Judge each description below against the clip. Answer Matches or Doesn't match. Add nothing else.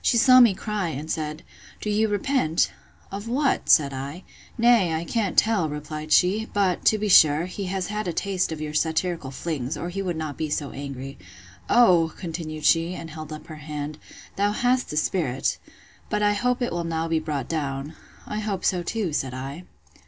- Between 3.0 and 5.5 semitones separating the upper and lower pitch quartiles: Matches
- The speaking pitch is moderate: Matches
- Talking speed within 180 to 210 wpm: Matches